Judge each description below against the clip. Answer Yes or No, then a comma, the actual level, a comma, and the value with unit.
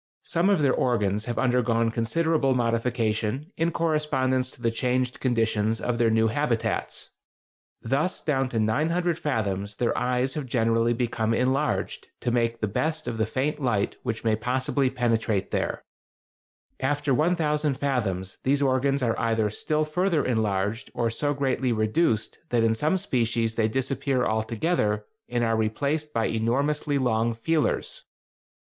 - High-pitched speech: No, low, 125 Hz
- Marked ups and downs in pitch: No, average, 4.1 semitones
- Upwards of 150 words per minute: No, average, 145 wpm